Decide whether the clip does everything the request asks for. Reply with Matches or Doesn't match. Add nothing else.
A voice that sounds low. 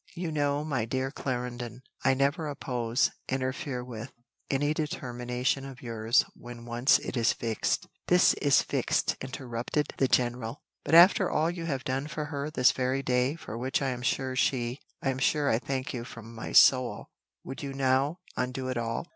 Matches